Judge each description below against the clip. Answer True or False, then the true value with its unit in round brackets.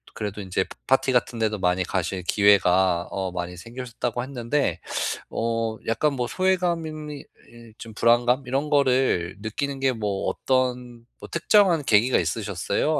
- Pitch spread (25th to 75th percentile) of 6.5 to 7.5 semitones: False (5.3 semitones)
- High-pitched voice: False (120 Hz)